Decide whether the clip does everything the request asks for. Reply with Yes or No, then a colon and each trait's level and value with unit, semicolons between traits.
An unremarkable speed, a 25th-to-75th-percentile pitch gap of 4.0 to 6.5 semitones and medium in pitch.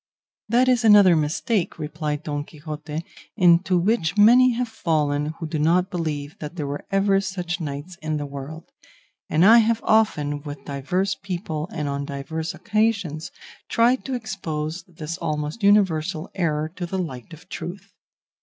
Yes: average, 155 wpm; average, 4.7 semitones; medium, 165 Hz